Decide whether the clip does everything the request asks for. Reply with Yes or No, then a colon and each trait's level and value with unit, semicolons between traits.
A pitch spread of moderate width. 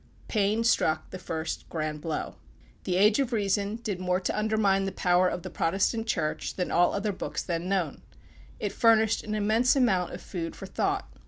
Yes: average, 3.4 semitones